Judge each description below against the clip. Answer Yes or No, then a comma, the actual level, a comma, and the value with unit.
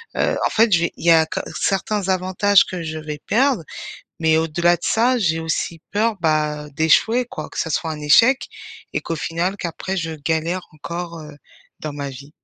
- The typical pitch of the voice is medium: Yes, medium, 170 Hz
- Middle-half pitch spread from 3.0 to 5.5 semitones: Yes, average, 3.5 semitones